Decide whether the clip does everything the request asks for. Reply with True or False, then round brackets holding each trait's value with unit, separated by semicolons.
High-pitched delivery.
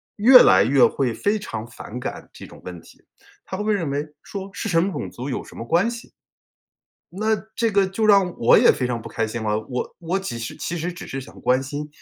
False (150 Hz)